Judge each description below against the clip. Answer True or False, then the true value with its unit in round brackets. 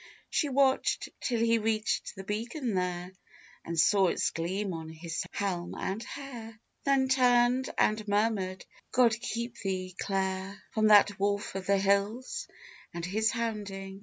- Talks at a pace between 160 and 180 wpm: False (145 wpm)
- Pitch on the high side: True (205 Hz)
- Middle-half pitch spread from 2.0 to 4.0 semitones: True (3.4 semitones)